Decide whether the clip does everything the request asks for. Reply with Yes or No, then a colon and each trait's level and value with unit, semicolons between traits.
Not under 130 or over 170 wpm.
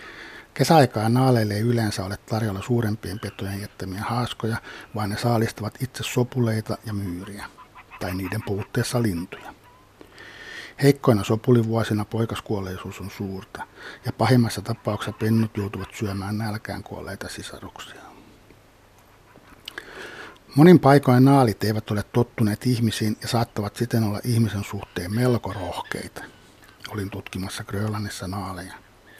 No: average, 110 wpm